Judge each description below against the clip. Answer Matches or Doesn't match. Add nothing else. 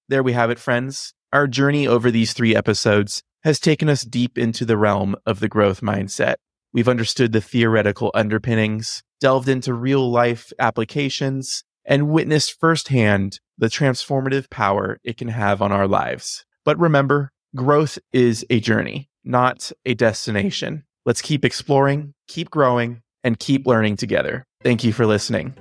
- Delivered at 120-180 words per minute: Matches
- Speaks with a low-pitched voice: Matches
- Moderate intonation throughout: Matches